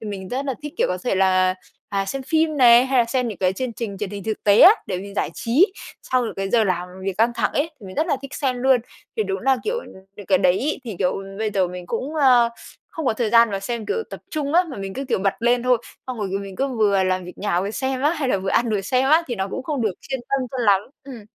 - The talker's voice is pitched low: No, high, 230 Hz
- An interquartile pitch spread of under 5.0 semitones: No, average, 5.3 semitones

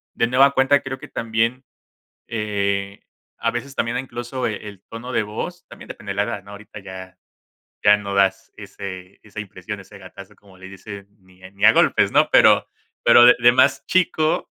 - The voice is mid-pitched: No, low, 105 Hz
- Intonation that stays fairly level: No, average, 3.7 semitones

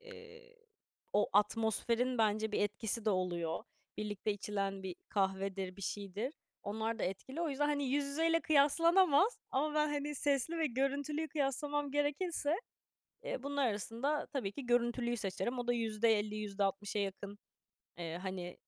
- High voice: Yes, high, 235 Hz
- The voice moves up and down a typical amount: No, wide, 6.2 semitones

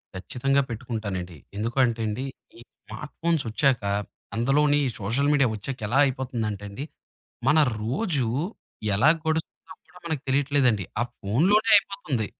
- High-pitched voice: No, low, 130 Hz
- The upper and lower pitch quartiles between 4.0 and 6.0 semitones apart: Yes, average, 4.7 semitones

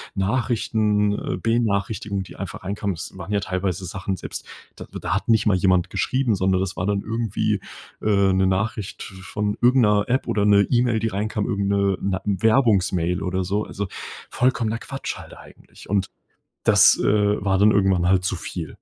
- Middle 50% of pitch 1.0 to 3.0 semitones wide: Yes, narrow, 2.4 semitones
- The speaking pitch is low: Yes, low, 100 Hz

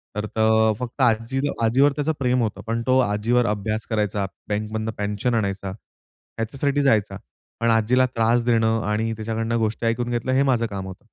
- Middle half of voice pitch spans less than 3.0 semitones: Yes, narrow, 2.4 semitones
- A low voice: Yes, low, 115 Hz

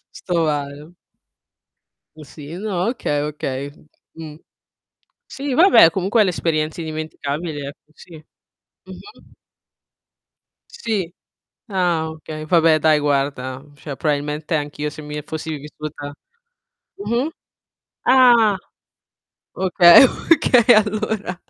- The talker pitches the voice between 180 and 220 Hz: No, medium, 160 Hz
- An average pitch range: Yes, average, 4.7 semitones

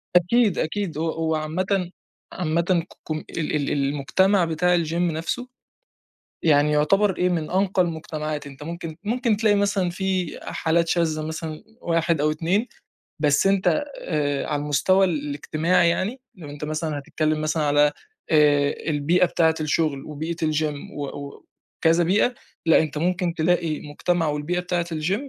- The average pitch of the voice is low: No, medium, 165 Hz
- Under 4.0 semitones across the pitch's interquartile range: Yes, average, 2.9 semitones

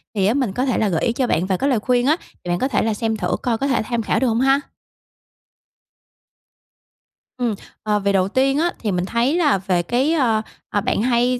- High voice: Yes, high, 235 Hz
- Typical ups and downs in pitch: Yes, average, 4.3 semitones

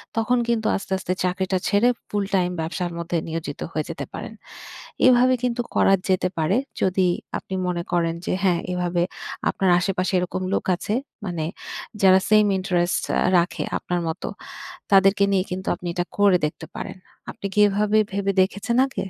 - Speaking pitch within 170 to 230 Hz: Yes, medium, 185 Hz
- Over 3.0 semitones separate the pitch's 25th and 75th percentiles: No, narrow, 2.4 semitones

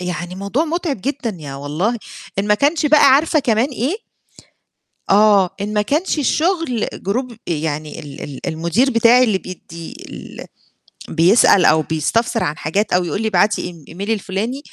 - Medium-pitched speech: No, high, 210 Hz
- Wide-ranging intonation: Yes, wide, 6.7 semitones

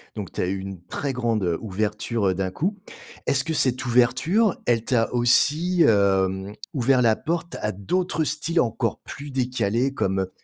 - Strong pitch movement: Yes, wide, 6.5 semitones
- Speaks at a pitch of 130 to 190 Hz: No, low, 120 Hz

